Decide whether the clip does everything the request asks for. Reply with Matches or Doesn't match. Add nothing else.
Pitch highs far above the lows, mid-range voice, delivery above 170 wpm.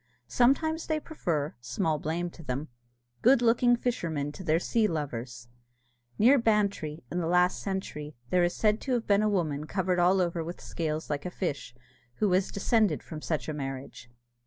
Matches